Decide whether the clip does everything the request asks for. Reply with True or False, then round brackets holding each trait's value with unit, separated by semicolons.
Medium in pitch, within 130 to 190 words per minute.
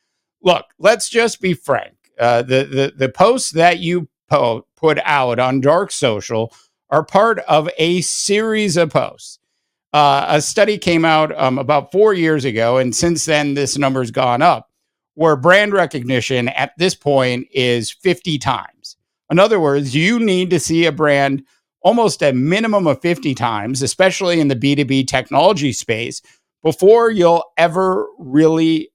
True (155 Hz; 165 wpm)